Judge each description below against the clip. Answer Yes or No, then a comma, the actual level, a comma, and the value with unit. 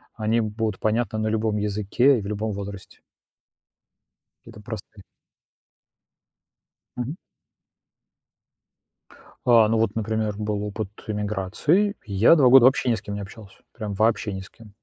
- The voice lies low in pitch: Yes, low, 110 Hz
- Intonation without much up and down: Yes, narrow, 1.9 semitones